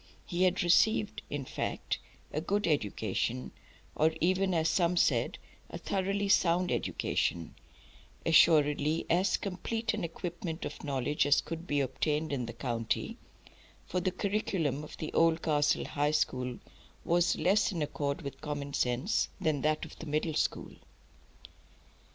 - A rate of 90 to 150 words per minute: Yes, average, 140 wpm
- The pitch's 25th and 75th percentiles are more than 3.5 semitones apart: Yes, average, 3.9 semitones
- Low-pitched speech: No, medium, 160 Hz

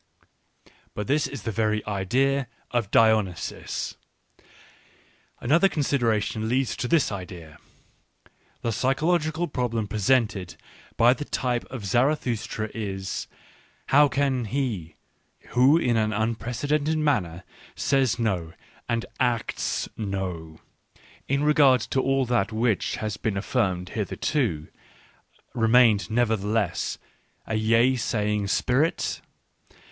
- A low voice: Yes, low, 115 Hz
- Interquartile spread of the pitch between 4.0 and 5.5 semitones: Yes, average, 4.3 semitones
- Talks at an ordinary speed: No, slow, 105 wpm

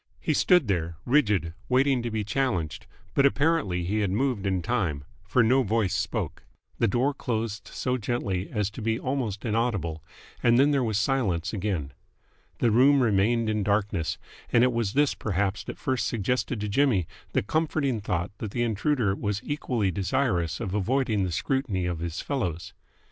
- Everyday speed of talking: Yes, average, 170 wpm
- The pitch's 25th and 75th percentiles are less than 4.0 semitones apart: No, average, 4.8 semitones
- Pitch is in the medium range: No, low, 110 Hz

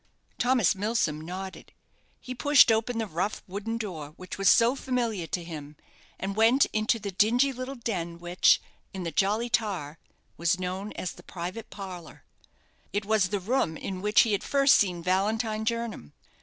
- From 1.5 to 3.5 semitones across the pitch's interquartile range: No, average, 4.1 semitones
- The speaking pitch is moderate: No, high, 205 Hz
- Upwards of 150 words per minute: Yes, average, 170 wpm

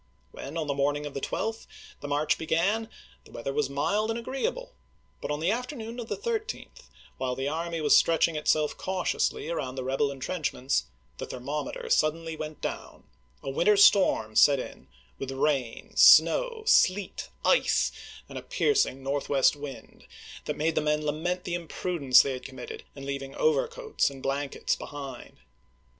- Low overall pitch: No, medium, 150 Hz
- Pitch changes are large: Yes, wide, 6.9 semitones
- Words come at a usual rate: Yes, average, 160 wpm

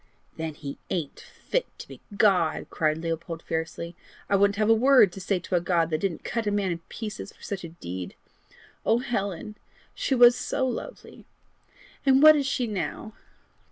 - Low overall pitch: No, high, 195 Hz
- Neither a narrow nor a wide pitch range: No, wide, 5.7 semitones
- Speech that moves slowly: No, average, 185 wpm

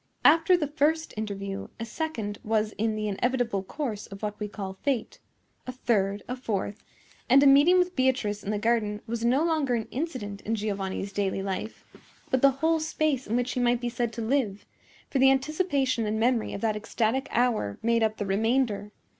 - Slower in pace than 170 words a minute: No, average, 195 wpm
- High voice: Yes, high, 230 Hz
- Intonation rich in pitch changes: No, average, 4.4 semitones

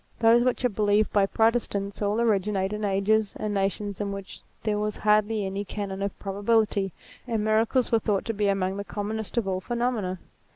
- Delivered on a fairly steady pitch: Yes, narrow, 1.9 semitones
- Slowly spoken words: No, average, 190 wpm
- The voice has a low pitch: No, high, 210 Hz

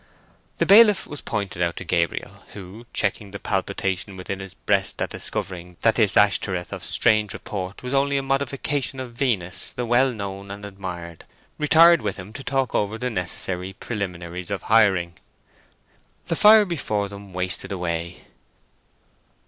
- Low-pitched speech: Yes, low, 100 Hz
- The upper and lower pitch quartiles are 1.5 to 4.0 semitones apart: No, average, 5.3 semitones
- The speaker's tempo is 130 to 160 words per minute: Yes, average, 155 wpm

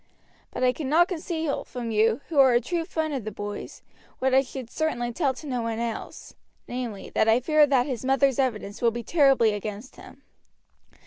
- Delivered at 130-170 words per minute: No, average, 195 wpm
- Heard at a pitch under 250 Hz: No, very high, 255 Hz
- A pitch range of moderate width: Yes, average, 3.9 semitones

